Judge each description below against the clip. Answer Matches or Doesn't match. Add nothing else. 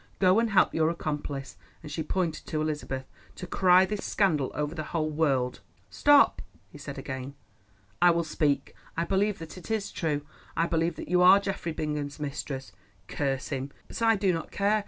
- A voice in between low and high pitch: Matches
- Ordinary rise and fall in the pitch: Matches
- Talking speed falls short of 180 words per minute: Doesn't match